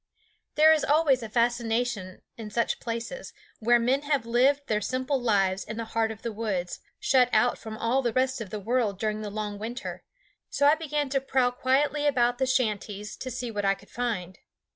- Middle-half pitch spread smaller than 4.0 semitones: Yes, average, 3.5 semitones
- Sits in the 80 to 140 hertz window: No, high, 240 Hz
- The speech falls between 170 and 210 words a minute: Yes, average, 200 wpm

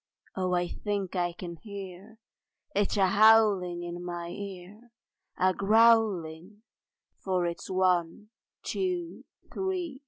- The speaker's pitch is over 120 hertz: Yes, high, 190 Hz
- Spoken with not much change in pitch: No, average, 3.6 semitones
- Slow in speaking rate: Yes, slow, 115 wpm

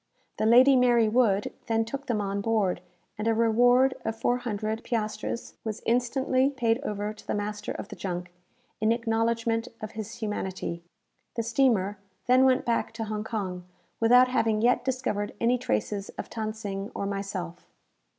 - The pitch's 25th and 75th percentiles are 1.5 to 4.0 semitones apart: Yes, average, 2.7 semitones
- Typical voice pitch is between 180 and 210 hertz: No, high, 225 Hz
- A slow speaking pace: No, average, 160 wpm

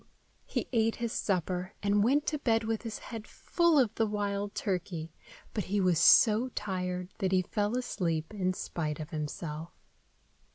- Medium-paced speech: Yes, average, 165 wpm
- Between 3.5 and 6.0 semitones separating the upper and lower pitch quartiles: Yes, average, 3.8 semitones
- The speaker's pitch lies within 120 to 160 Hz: No, high, 200 Hz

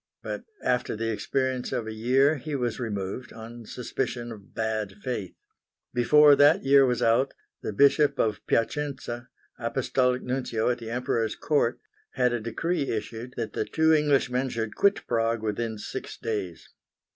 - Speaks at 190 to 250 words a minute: No, average, 155 wpm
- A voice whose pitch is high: No, low, 120 Hz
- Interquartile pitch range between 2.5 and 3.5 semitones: Yes, average, 3.1 semitones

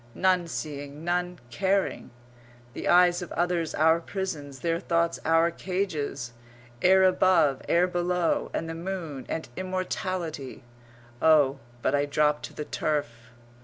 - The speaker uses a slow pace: Yes, slow, 130 wpm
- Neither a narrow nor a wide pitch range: Yes, average, 3.3 semitones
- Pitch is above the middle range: No, medium, 165 Hz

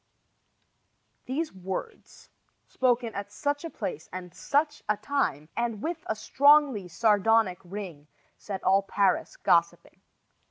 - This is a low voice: No, high, 220 Hz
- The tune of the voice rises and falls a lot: Yes, wide, 6.9 semitones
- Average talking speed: No, slow, 120 wpm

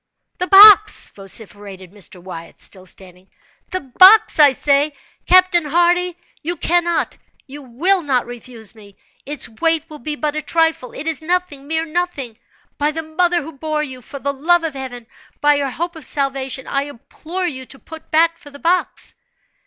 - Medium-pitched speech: No, very high, 295 Hz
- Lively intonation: No, average, 4.7 semitones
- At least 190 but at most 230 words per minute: No, average, 160 wpm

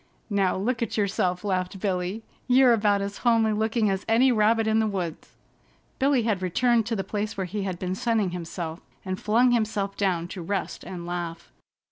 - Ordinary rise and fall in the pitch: Yes, average, 3.4 semitones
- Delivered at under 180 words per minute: No, average, 185 wpm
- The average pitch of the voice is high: Yes, high, 205 Hz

